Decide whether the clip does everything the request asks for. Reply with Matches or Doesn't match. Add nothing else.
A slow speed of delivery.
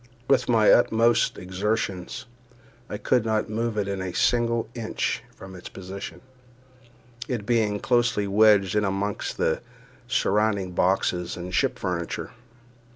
Matches